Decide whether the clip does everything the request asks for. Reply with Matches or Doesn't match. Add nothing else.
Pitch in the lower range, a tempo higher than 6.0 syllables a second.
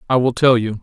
Matches